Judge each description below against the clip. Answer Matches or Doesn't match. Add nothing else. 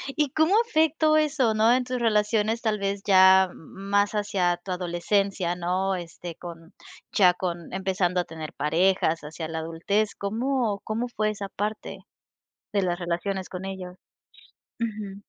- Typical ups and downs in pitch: Matches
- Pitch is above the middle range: Matches